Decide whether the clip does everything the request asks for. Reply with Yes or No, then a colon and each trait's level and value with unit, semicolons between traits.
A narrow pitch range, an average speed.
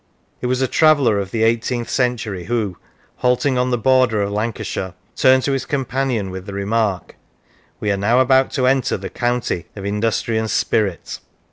No: average, 4.0 semitones; average, 180 wpm